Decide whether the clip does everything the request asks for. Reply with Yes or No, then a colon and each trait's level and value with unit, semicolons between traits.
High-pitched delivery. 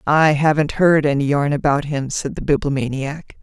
No: medium, 145 Hz